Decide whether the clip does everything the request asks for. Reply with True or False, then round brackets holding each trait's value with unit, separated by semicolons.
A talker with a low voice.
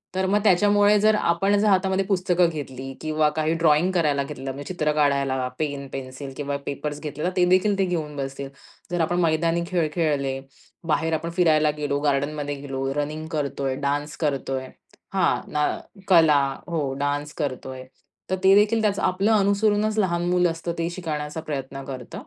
False (155 Hz)